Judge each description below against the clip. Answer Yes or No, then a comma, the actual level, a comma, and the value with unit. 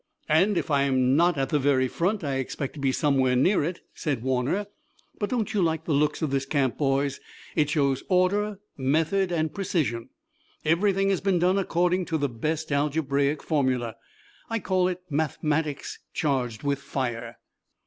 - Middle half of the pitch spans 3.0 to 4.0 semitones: No, average, 4.8 semitones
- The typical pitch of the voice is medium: Yes, medium, 150 Hz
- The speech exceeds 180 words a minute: No, average, 165 wpm